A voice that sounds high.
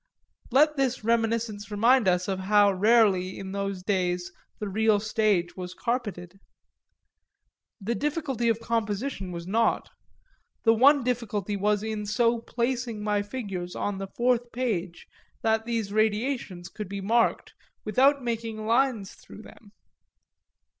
Yes: high, 215 Hz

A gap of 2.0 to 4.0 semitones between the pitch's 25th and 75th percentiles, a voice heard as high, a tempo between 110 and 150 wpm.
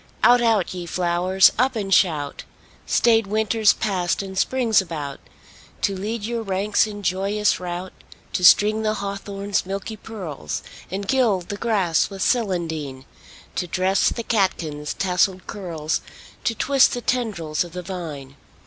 Yes: average, 3.6 semitones; high, 195 Hz; average, 145 wpm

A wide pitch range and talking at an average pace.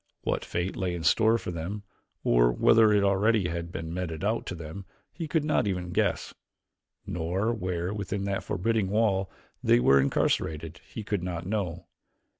No: average, 3.8 semitones; average, 170 wpm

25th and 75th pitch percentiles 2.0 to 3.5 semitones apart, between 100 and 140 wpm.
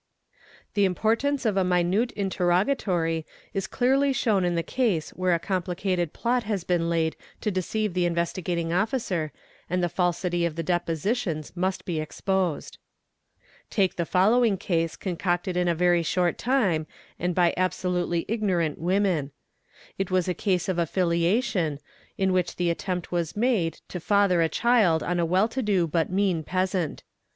No: average, 2.8 semitones; average, 160 wpm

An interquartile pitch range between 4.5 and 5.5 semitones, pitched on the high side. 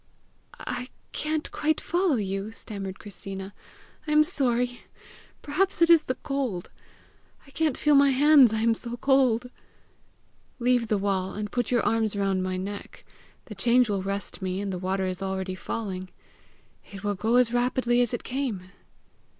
Yes: average, 4.9 semitones; high, 225 Hz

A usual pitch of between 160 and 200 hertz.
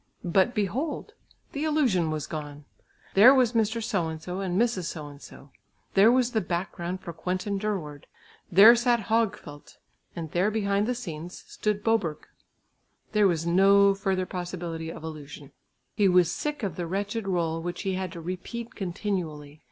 Yes: medium, 185 Hz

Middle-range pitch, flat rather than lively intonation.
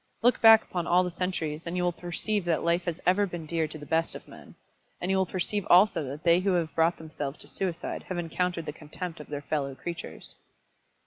Yes: medium, 175 Hz; narrow, 2.3 semitones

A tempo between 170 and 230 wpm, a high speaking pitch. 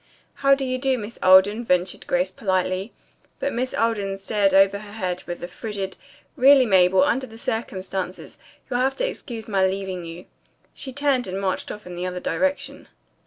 Yes: average, 185 wpm; high, 200 Hz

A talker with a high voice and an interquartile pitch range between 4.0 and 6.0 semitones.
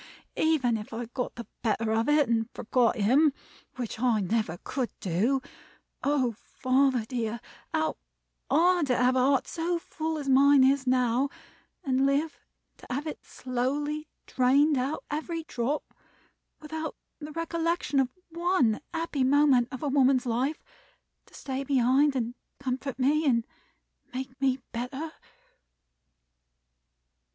No: very high, 265 Hz; average, 3.3 semitones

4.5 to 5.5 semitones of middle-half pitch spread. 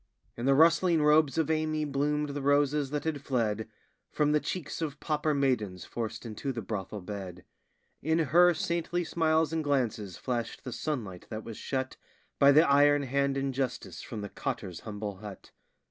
Yes: average, 5.2 semitones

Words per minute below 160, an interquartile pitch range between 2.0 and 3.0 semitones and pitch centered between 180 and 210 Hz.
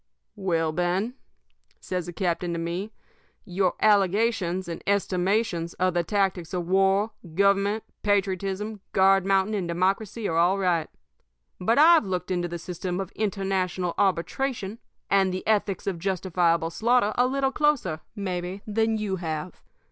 Yes: average, 140 wpm; narrow, 2.6 semitones; high, 190 Hz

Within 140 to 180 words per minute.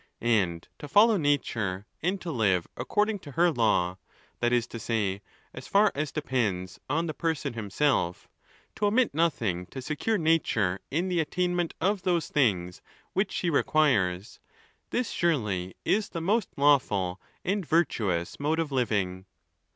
Yes: average, 150 wpm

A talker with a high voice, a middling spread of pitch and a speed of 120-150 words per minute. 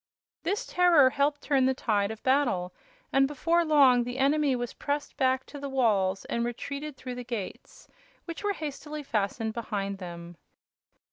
No: very high, 260 Hz; average, 4.7 semitones; average, 160 wpm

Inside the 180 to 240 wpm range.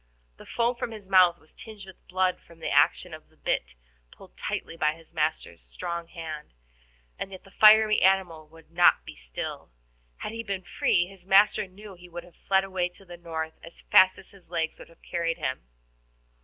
Yes: average, 200 wpm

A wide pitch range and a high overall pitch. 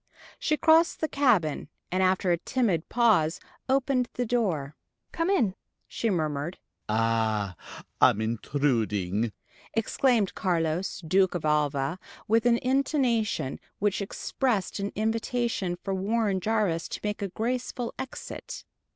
Yes: wide, 7.3 semitones; high, 195 Hz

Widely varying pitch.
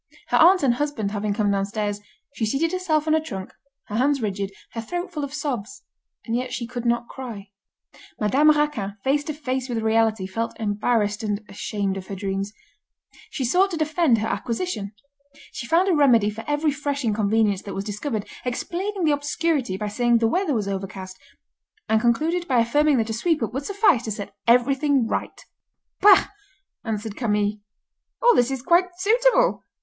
Yes: wide, 6.1 semitones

